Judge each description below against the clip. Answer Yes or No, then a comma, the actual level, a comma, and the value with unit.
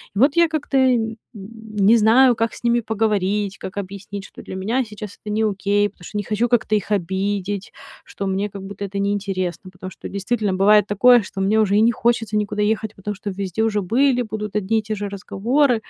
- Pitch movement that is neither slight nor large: No, narrow, 2.2 semitones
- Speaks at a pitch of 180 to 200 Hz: No, high, 210 Hz